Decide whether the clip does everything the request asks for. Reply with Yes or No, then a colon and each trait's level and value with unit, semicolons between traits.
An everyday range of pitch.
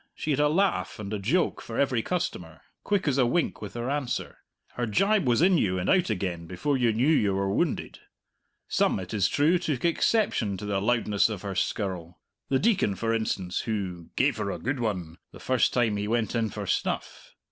No: wide, 6.5 semitones